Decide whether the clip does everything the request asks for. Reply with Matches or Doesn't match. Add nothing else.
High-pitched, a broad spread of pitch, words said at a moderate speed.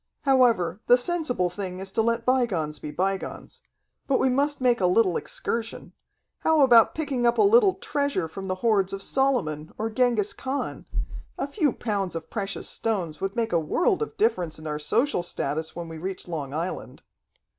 Matches